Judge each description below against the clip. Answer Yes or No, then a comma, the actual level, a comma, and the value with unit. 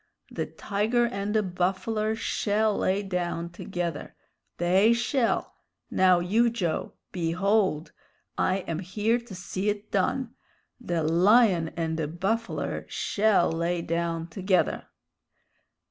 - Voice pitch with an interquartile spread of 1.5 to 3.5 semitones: No, average, 4.0 semitones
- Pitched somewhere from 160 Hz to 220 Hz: Yes, high, 190 Hz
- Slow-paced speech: Yes, slow, 115 wpm